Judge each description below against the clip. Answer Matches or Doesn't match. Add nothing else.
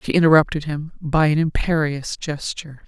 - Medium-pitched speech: Matches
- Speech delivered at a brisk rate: Doesn't match